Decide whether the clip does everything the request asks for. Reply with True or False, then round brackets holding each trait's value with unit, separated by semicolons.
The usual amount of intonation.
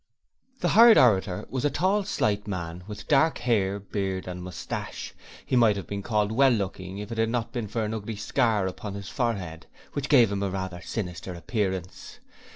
True (4.0 semitones)